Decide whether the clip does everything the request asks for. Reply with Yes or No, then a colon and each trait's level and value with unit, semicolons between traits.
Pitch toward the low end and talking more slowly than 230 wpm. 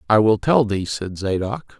Yes: low, 110 Hz; average, 200 wpm